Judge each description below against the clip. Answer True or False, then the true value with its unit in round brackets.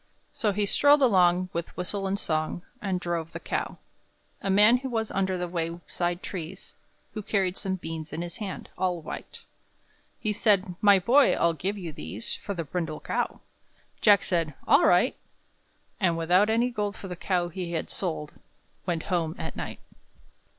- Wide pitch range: False (3.2 semitones)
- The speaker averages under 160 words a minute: False (170 wpm)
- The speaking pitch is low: False (185 Hz)